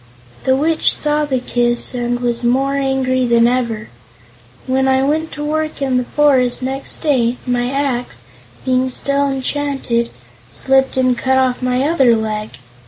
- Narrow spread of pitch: Yes, narrow, 2.2 semitones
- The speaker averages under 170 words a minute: Yes, average, 155 wpm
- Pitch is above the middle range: Yes, very high, 260 Hz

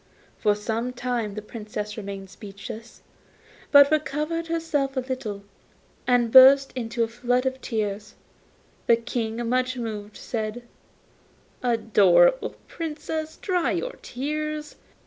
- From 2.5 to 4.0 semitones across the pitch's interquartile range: No, average, 4.8 semitones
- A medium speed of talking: No, slow, 115 wpm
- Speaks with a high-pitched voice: Yes, high, 245 Hz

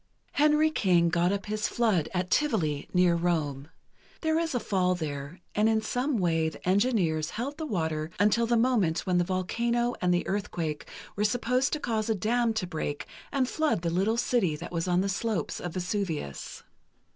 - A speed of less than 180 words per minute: No, average, 185 wpm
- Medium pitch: No, high, 195 Hz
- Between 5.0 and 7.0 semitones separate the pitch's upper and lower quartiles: Yes, wide, 5.6 semitones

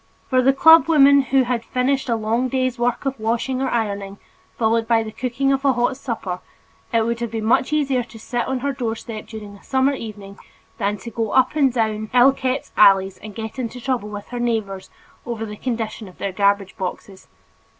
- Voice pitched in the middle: No, high, 235 Hz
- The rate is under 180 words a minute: No, fast, 205 wpm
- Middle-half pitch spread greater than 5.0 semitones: No, average, 3.3 semitones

